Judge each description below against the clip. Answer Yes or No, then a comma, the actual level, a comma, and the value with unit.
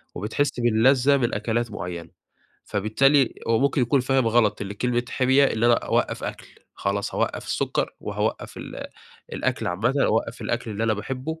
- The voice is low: Yes, low, 120 Hz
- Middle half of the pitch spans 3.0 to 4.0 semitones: Yes, average, 3.5 semitones